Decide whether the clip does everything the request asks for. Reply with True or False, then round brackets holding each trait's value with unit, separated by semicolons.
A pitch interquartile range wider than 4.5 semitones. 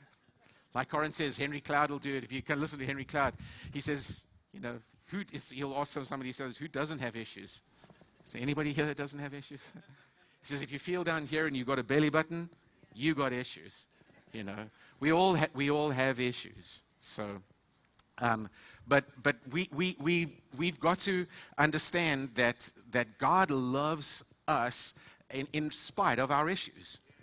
False (3.4 semitones)